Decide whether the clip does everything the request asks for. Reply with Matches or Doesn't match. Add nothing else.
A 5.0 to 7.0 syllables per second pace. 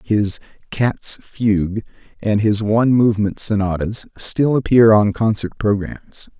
Doesn't match